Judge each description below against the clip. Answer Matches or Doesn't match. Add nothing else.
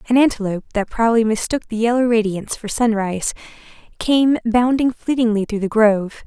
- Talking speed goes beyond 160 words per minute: Doesn't match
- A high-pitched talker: Matches